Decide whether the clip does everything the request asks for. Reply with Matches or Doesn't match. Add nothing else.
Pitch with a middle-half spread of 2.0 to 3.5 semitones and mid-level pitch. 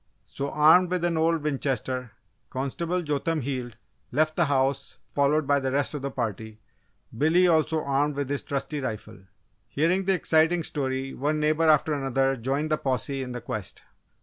Matches